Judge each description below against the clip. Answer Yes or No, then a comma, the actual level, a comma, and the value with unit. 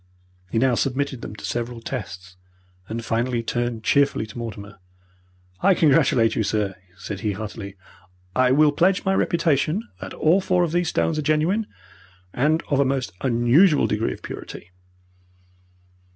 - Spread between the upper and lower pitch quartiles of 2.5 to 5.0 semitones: No, wide, 5.6 semitones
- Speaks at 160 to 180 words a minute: No, average, 150 wpm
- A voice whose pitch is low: Yes, low, 130 Hz